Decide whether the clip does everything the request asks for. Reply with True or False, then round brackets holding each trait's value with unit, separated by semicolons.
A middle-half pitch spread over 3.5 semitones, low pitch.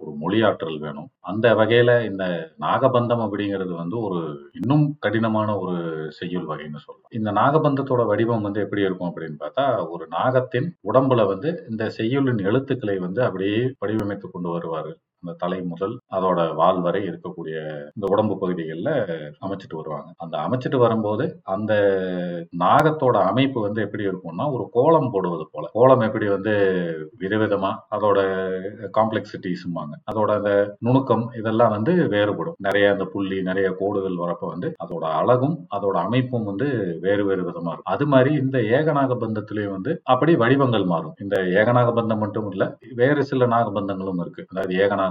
True (4.5 semitones; 105 Hz)